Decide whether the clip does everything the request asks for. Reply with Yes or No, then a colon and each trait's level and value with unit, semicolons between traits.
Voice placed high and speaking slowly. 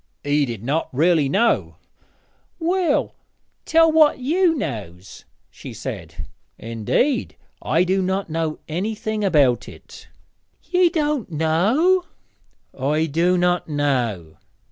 No: medium, 175 Hz; slow, 110 wpm